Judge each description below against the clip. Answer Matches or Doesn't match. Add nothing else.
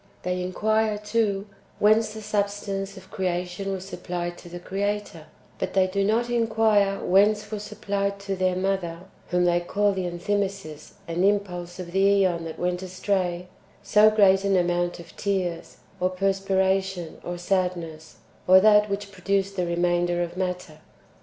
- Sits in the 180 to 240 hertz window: Matches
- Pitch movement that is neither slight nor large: Doesn't match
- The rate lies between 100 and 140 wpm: Doesn't match